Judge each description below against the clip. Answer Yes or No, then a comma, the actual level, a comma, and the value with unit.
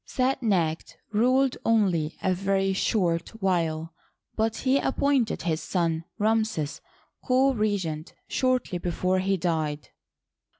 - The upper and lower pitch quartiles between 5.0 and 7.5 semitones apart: Yes, average, 5.3 semitones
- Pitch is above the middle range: Yes, high, 195 Hz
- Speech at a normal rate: No, slow, 120 wpm